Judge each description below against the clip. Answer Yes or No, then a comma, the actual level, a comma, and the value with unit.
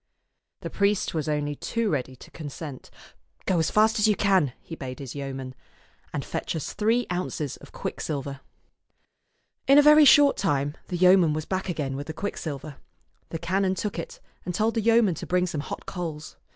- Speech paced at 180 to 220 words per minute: Yes, average, 195 wpm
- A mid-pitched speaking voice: Yes, medium, 170 Hz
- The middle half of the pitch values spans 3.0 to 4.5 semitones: No, wide, 5.6 semitones